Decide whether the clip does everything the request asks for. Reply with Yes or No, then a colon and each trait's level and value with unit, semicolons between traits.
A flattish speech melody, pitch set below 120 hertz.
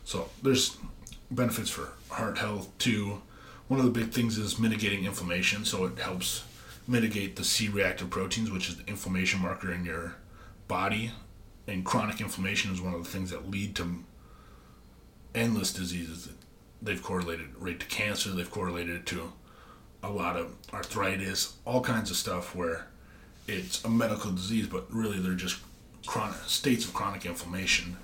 No: average, 3.3 semitones; very low, 95 Hz